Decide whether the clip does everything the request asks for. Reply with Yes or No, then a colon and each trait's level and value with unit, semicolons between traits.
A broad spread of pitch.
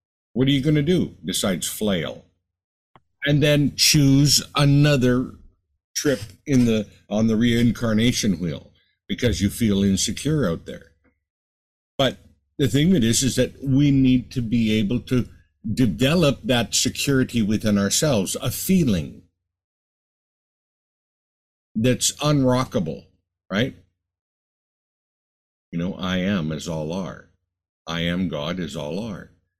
Yes: wide, 6.4 semitones